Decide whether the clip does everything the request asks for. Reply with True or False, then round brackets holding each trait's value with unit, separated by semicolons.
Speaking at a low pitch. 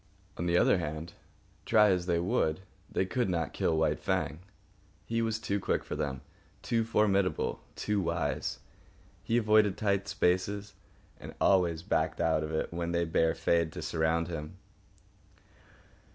True (85 Hz)